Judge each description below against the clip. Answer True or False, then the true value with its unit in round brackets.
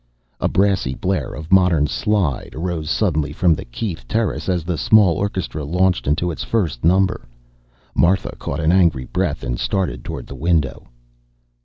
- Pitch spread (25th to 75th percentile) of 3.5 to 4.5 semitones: True (4.2 semitones)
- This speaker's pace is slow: False (160 wpm)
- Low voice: True (85 Hz)